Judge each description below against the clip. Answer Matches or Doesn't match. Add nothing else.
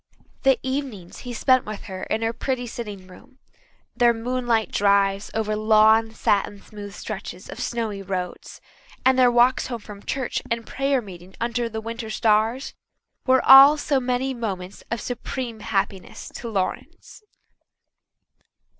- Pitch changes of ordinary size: Matches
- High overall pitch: Matches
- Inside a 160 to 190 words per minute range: Doesn't match